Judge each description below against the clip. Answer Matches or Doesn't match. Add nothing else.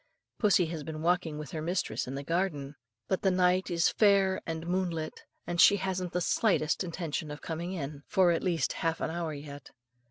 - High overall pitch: Doesn't match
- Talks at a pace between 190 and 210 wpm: Matches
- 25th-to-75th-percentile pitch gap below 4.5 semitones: Matches